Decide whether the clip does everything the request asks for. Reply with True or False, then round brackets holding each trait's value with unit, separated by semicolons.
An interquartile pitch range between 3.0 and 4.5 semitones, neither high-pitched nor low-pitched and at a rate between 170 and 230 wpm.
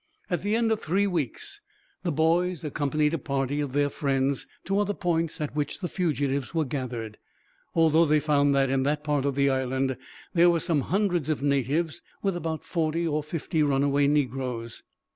True (3.5 semitones; 150 Hz; 180 wpm)